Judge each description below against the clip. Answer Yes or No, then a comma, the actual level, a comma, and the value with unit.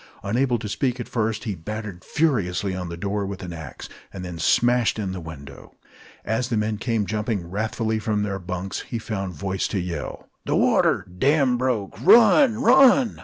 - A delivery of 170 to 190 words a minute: Yes, average, 180 wpm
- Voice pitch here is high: No, low, 105 Hz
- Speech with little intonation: No, average, 4.6 semitones